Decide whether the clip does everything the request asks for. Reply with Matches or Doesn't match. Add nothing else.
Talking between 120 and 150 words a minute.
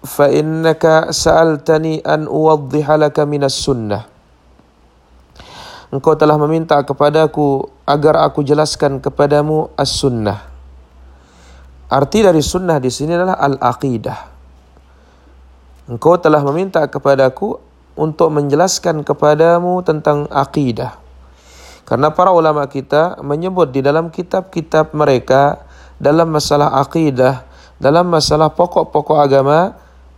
Doesn't match